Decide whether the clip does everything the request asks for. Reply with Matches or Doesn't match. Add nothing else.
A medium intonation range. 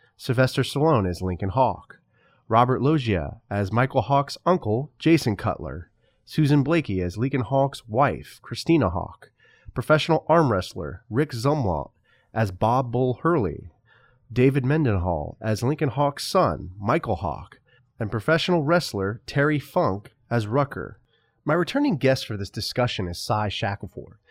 Doesn't match